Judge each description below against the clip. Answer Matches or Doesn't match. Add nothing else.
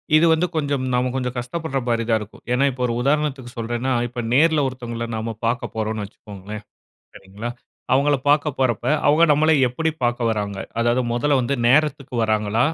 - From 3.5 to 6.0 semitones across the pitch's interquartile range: Matches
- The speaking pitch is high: Doesn't match